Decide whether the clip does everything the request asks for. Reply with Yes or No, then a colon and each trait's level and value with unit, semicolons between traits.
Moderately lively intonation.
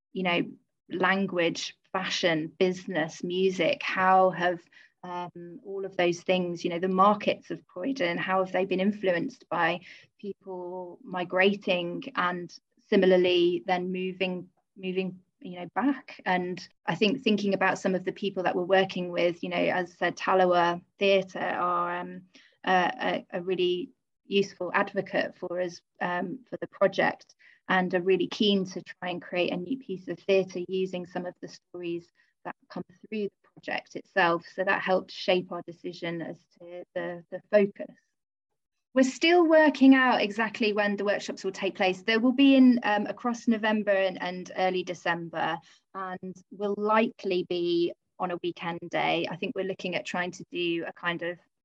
No: narrow, 2.0 semitones